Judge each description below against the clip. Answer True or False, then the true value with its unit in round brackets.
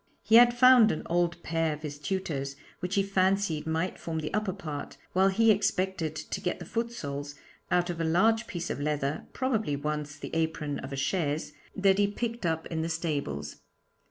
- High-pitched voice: False (165 Hz)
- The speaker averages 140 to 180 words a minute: False (195 wpm)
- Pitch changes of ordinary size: True (4.7 semitones)